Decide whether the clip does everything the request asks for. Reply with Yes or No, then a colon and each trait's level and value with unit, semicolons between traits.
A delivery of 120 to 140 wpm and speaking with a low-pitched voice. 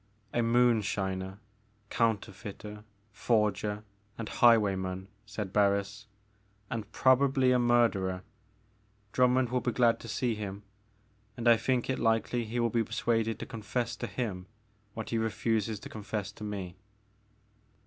Yes: slow, 135 wpm; low, 110 Hz